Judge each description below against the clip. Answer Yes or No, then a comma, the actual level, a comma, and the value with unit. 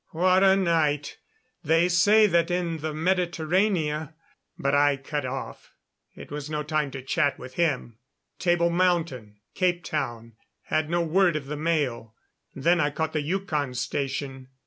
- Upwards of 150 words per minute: No, average, 145 wpm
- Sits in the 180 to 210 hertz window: No, medium, 155 Hz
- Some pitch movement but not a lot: Yes, average, 3.8 semitones